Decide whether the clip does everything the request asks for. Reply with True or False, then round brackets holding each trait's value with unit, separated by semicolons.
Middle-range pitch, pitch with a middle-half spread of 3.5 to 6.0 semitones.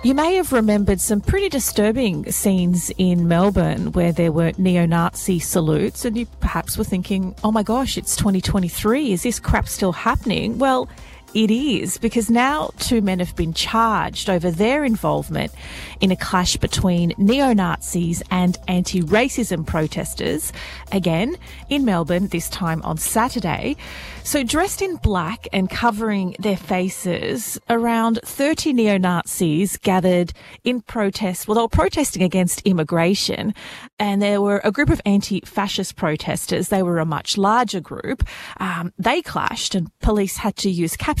False (200 Hz; 4.3 semitones)